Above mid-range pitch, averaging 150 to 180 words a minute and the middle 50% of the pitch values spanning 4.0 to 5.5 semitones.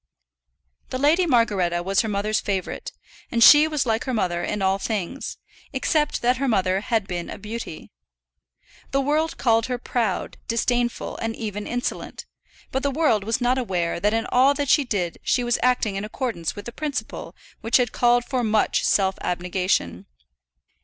Yes: high, 230 Hz; average, 175 wpm; average, 4.6 semitones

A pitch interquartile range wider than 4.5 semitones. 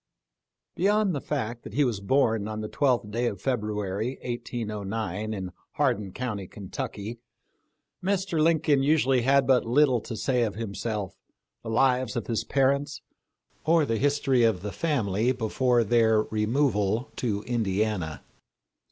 No: average, 4.2 semitones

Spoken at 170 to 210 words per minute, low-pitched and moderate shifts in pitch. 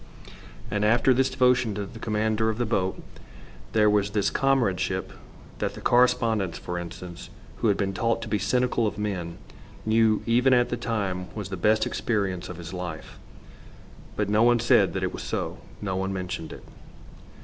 Yes: average, 180 wpm; low, 105 Hz; average, 3.7 semitones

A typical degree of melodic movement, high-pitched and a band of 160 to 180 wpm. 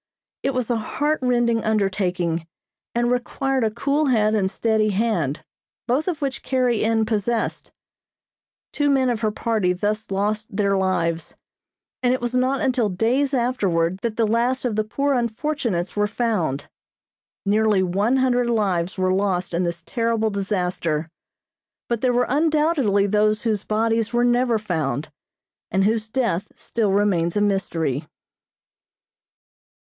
No: average, 4.2 semitones; high, 220 Hz; average, 145 wpm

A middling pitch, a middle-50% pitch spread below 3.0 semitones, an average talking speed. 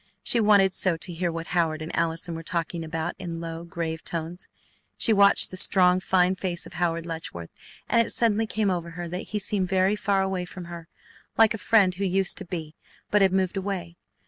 No: medium, 180 Hz; narrow, 2.6 semitones; fast, 210 wpm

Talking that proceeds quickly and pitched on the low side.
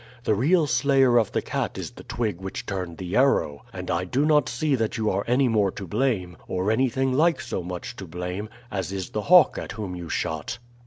Yes: fast, 220 wpm; low, 105 Hz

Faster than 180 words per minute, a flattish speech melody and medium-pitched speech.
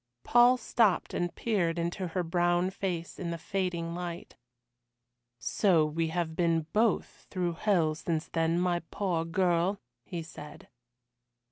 No: slow, 135 wpm; narrow, 2.0 semitones; medium, 175 Hz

